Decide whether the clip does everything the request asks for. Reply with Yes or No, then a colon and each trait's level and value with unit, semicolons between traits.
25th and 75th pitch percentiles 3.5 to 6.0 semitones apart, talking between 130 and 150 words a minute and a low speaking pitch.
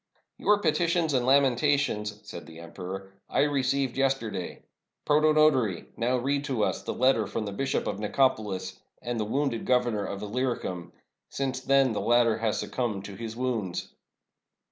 No: average, 4.5 semitones; average, 165 wpm; low, 125 Hz